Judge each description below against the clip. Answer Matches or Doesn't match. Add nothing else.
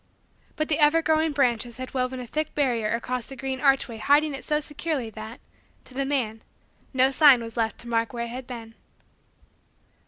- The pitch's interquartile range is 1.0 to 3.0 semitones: Doesn't match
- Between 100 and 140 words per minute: Doesn't match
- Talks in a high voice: Matches